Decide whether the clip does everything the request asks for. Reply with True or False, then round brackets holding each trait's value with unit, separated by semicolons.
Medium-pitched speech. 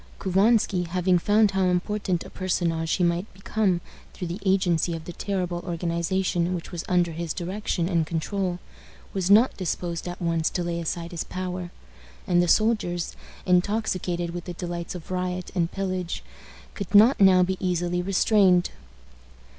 True (180 Hz)